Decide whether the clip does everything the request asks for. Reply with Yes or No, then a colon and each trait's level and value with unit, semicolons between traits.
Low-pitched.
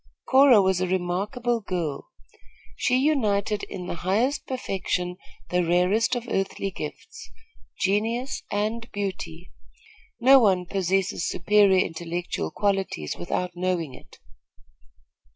No: high, 195 Hz